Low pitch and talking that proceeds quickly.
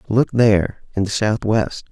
No: low, 105 Hz; average, 155 wpm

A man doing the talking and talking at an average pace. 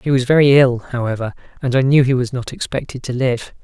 No: male; fast, 230 wpm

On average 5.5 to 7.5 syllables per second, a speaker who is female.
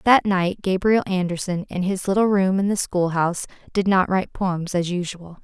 No: 4.9 syllables/s; female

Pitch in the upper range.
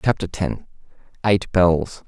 No: very low, 95 Hz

